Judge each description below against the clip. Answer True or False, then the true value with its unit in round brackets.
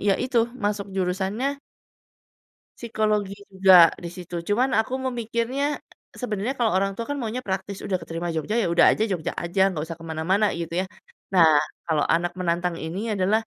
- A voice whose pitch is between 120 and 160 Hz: False (195 Hz)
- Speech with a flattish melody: False (4.2 semitones)